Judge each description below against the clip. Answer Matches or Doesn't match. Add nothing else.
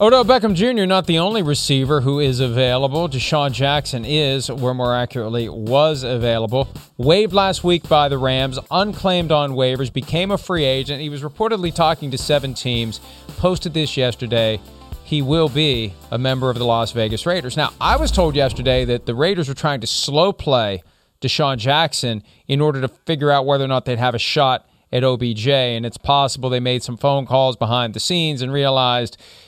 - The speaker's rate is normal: Matches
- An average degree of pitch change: Matches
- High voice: Doesn't match